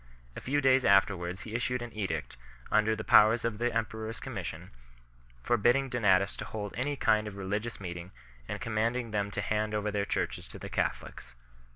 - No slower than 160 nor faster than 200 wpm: Yes, average, 185 wpm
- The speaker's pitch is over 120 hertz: No, low, 110 Hz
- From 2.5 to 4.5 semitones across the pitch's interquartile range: Yes, average, 2.8 semitones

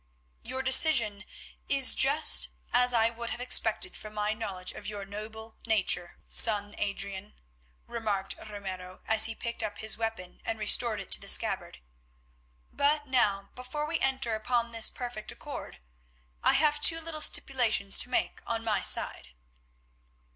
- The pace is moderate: Yes, average, 155 wpm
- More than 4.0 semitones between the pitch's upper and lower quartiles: No, average, 3.5 semitones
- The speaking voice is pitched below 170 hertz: No, high, 225 Hz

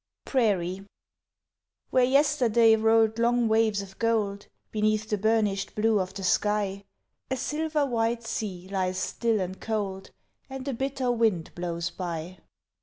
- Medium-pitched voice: No, high, 215 Hz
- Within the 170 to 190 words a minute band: No, slow, 135 wpm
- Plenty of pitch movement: No, average, 3.4 semitones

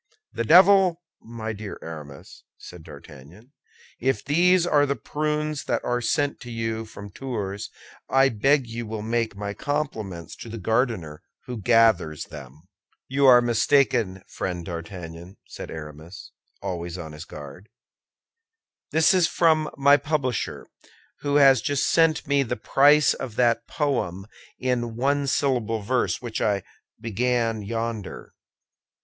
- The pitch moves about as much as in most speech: No, wide, 6.2 semitones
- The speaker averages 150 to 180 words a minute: No, slow, 135 wpm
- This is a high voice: No, low, 115 Hz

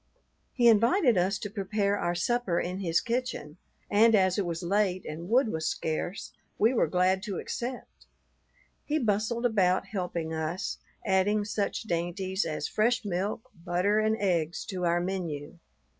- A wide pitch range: No, average, 3.7 semitones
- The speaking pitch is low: No, high, 190 Hz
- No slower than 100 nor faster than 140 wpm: No, average, 155 wpm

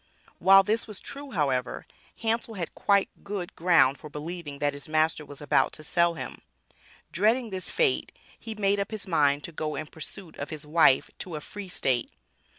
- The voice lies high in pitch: No, medium, 170 Hz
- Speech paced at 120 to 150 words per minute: No, average, 185 wpm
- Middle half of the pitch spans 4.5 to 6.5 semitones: Yes, average, 5.2 semitones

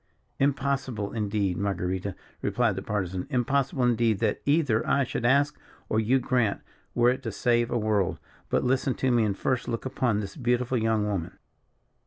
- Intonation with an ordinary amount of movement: Yes, average, 3.9 semitones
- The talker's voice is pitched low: Yes, low, 120 Hz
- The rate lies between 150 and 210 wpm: Yes, average, 170 wpm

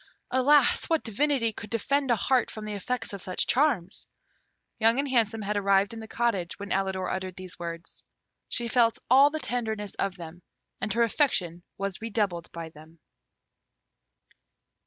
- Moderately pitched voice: No, high, 215 Hz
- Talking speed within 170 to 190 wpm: No, average, 160 wpm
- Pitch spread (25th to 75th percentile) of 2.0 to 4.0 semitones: No, average, 4.6 semitones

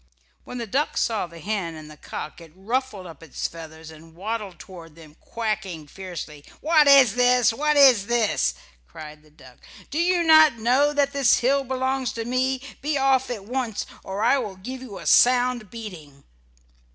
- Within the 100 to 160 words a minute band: No, average, 180 wpm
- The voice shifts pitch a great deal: Yes, wide, 7.7 semitones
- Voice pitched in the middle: No, high, 225 Hz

